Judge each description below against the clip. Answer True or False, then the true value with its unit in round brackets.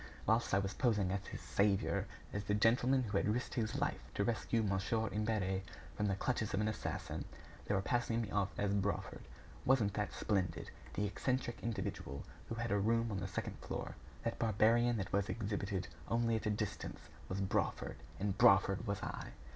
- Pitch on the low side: True (105 Hz)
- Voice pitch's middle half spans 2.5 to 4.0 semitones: True (2.8 semitones)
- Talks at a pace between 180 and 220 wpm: True (185 wpm)